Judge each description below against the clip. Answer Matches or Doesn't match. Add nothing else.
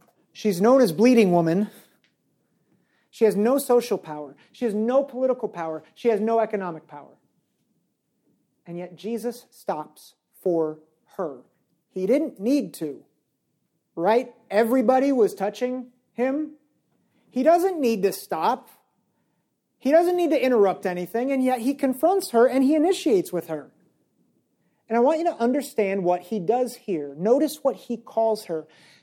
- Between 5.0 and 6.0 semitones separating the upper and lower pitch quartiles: Matches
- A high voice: Matches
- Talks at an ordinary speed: Matches